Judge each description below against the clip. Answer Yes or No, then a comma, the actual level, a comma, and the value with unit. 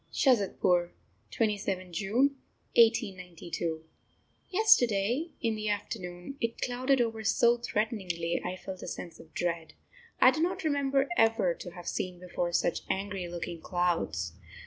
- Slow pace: Yes, slow, 130 wpm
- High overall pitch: Yes, high, 195 Hz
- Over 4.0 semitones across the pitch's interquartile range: Yes, average, 5.2 semitones